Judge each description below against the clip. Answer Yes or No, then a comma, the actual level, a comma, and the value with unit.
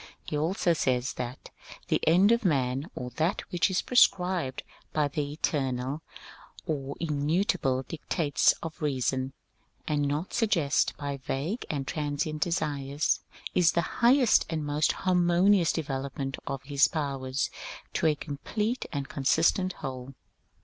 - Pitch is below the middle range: No, medium, 150 Hz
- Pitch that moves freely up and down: No, average, 4.0 semitones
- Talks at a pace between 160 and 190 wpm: No, average, 140 wpm